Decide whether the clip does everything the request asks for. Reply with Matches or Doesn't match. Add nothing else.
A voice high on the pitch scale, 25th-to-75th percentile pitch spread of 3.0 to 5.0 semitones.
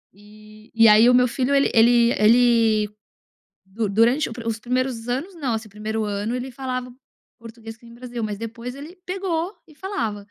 Doesn't match